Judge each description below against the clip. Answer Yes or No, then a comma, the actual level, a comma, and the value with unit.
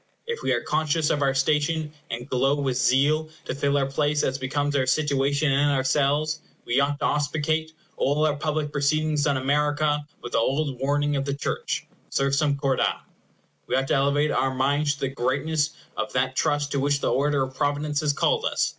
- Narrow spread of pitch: Yes, narrow, 1.7 semitones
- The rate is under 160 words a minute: No, average, 195 wpm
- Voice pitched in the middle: Yes, medium, 145 Hz